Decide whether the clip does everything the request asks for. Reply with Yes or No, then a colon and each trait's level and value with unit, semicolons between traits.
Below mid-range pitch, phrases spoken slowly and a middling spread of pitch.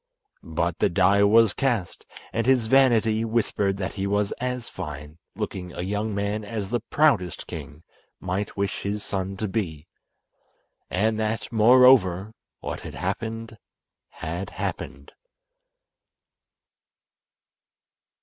Yes: low, 105 Hz; slow, 120 wpm; average, 3.4 semitones